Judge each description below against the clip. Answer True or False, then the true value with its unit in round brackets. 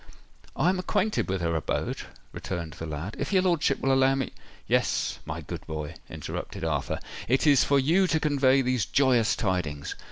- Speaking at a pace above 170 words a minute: True (180 wpm)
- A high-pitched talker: False (130 Hz)